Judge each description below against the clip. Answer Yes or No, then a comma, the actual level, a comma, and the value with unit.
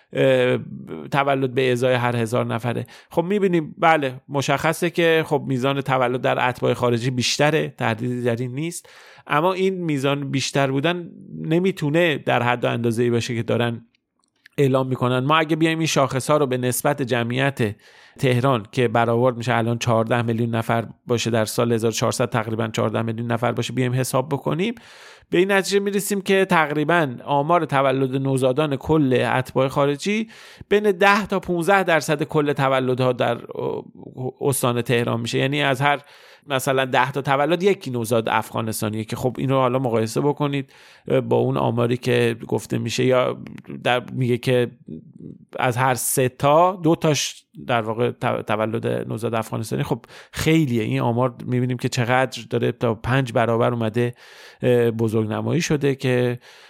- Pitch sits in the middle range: No, low, 130 Hz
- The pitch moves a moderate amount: Yes, average, 3.4 semitones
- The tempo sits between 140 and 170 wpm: Yes, average, 150 wpm